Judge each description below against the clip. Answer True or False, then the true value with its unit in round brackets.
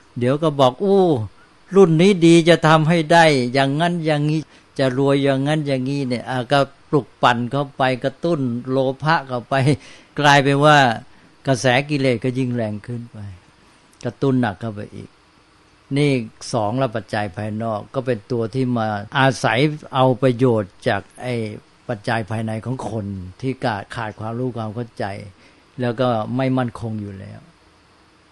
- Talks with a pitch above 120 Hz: True (130 Hz)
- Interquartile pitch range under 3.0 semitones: False (3.8 semitones)